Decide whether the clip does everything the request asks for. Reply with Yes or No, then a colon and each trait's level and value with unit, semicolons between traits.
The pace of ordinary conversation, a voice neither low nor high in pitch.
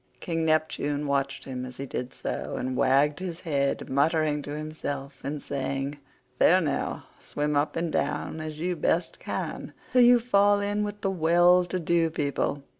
Yes: average, 170 wpm; medium, 155 Hz